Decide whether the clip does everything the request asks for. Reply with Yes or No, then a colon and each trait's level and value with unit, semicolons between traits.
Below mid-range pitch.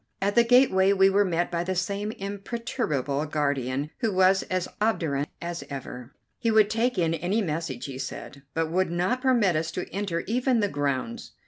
No: medium, 185 Hz